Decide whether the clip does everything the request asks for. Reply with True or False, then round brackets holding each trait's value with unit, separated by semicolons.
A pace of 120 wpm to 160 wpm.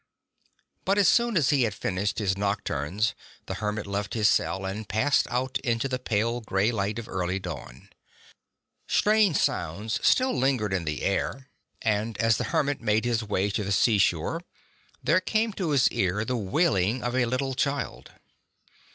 False (170 wpm)